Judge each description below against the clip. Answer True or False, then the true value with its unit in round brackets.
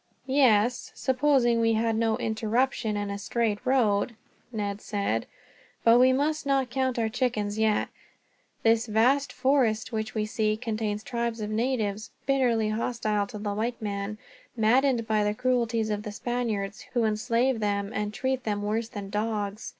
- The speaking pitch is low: False (225 Hz)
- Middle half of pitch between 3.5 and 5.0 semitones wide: False (2.8 semitones)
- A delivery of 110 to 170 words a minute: True (160 wpm)